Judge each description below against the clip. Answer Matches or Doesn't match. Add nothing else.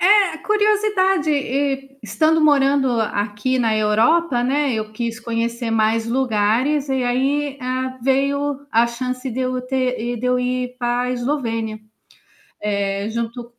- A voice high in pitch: Matches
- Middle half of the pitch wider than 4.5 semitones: Doesn't match